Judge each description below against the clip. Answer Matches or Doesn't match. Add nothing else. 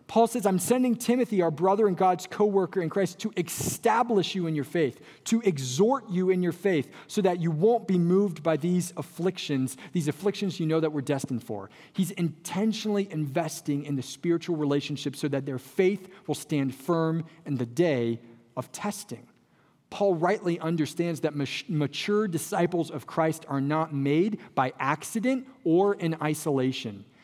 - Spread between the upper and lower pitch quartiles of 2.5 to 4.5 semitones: Doesn't match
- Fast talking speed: Doesn't match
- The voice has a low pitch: Doesn't match